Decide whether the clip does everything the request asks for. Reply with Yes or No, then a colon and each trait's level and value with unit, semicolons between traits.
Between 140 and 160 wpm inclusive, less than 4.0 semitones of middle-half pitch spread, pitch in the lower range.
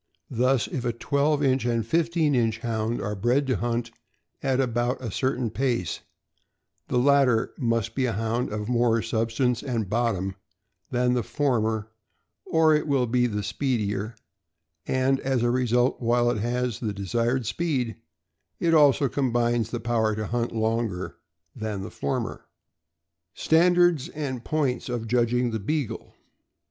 Yes: average, 150 wpm; average, 2.8 semitones; low, 120 Hz